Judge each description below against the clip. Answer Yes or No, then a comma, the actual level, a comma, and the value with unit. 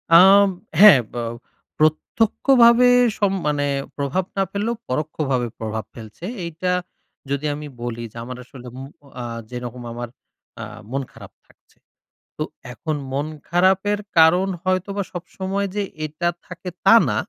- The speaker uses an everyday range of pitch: No, wide, 6.9 semitones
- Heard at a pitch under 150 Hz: No, medium, 160 Hz